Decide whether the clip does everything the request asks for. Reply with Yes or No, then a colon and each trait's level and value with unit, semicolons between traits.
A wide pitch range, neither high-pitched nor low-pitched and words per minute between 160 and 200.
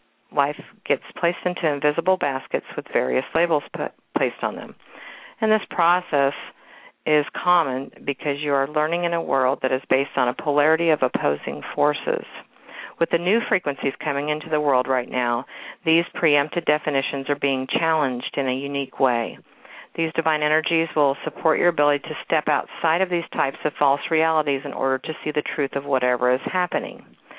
No: average, 3.1 semitones; medium, 150 Hz; average, 175 wpm